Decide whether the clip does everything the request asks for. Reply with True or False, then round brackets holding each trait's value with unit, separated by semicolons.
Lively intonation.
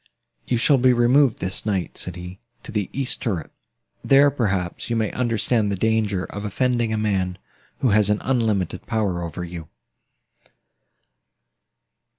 False (4.4 semitones)